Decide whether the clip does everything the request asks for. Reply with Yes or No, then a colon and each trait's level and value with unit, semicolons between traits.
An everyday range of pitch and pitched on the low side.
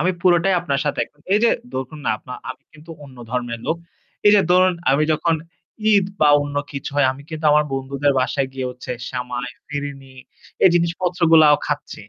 No: average, 4.3 semitones; medium, 145 Hz